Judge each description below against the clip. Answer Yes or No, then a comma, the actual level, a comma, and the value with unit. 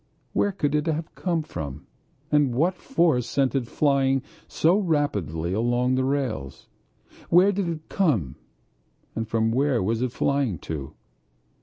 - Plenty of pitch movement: Yes, wide, 5.8 semitones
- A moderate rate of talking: Yes, average, 145 wpm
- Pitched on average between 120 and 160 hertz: Yes, low, 135 Hz